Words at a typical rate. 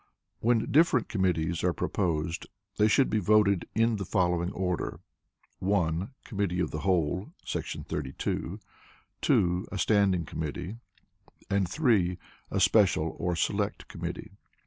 No: slow, 125 wpm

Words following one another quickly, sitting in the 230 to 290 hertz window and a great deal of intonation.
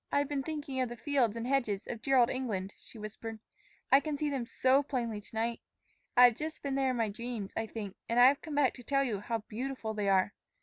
No: fast, 250 wpm; high, 245 Hz; average, 3.7 semitones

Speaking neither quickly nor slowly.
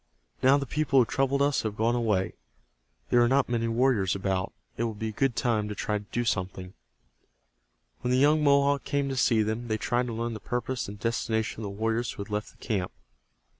No: fast, 220 wpm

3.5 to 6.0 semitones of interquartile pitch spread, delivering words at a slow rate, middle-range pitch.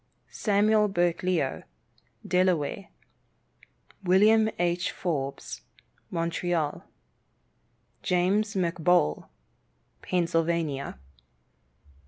No: narrow, 2.4 semitones; slow, 50 wpm; medium, 175 Hz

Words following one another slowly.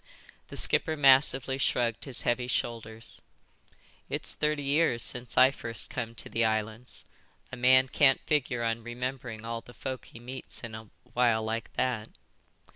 No: average, 155 wpm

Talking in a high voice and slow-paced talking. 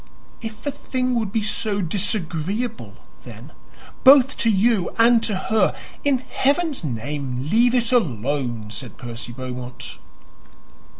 Yes: high, 210 Hz; slow, 125 wpm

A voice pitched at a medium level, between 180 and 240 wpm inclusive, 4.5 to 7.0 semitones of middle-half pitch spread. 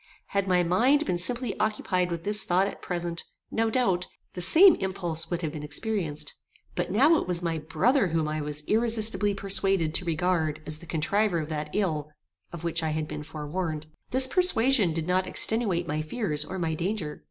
Yes: medium, 180 Hz; average, 190 wpm; average, 5.0 semitones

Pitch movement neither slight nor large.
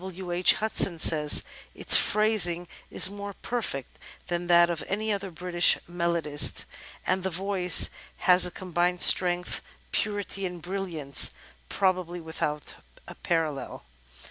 No: narrow, 2.0 semitones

